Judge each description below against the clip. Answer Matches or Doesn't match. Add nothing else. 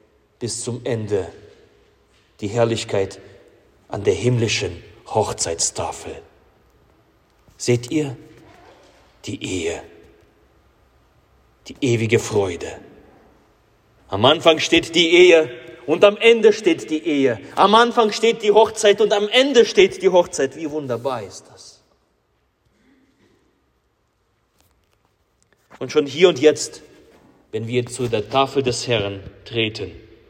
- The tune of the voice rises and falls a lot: Matches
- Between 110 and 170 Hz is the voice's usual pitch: Matches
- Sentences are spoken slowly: Matches